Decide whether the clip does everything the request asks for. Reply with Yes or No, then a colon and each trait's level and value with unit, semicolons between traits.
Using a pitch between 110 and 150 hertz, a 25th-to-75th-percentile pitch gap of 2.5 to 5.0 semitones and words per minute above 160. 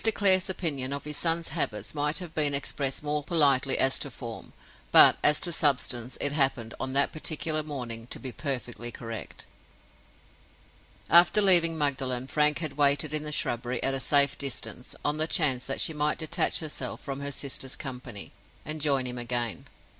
Yes: medium, 140 Hz; average, 3.0 semitones; average, 175 wpm